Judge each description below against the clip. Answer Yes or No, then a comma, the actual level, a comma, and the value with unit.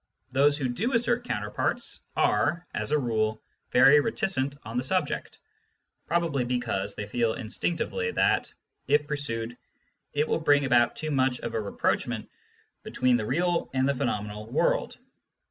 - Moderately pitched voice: No, low, 130 Hz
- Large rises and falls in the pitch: No, average, 4.7 semitones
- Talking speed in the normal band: Yes, average, 150 wpm